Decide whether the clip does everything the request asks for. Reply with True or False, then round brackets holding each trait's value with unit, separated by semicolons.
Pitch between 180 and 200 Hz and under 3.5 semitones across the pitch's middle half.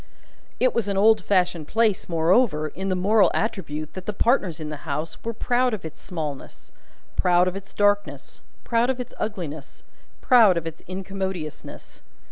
False (190 Hz; 4.8 semitones)